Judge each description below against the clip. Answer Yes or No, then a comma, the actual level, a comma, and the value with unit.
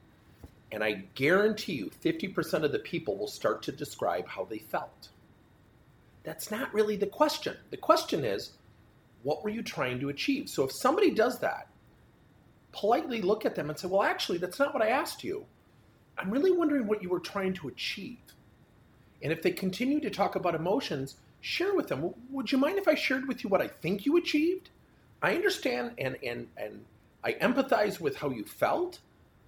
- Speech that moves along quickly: No, average, 185 wpm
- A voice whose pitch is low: No, high, 210 Hz